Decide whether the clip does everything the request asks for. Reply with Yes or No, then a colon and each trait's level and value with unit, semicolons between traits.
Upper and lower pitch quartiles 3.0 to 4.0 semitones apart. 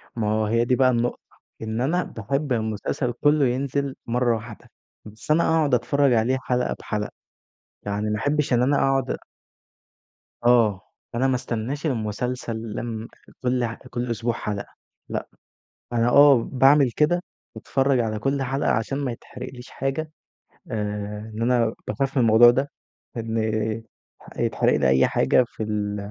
Yes: average, 3.5 semitones